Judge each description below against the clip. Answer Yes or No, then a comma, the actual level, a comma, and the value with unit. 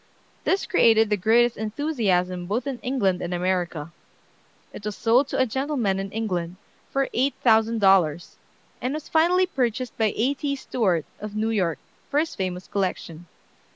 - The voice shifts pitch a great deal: Yes, wide, 5.8 semitones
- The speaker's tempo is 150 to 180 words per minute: Yes, average, 160 wpm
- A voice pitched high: Yes, high, 220 Hz